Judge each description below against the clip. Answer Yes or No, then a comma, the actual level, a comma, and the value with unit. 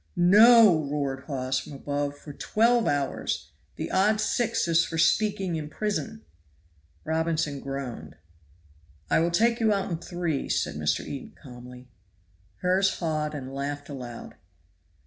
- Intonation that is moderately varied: No, wide, 5.8 semitones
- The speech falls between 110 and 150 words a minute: Yes, slow, 135 wpm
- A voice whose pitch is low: No, medium, 155 Hz